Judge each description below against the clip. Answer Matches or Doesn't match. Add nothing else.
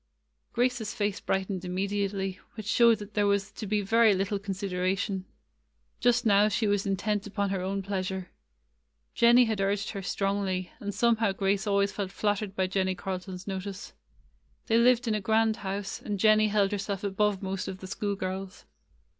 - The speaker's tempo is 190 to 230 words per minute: Doesn't match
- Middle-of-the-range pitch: Doesn't match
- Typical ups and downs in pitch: Doesn't match